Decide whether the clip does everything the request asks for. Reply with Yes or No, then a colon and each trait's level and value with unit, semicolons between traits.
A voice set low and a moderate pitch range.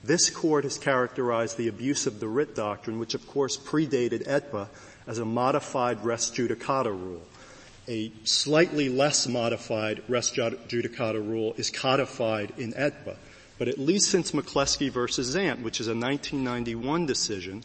Yes: low, 120 Hz; average, 3.8 semitones